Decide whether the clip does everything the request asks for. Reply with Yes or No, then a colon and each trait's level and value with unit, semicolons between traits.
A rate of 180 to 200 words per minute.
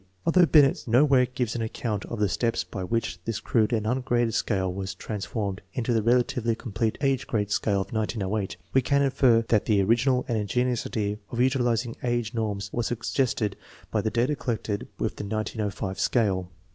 Yes: average, 185 wpm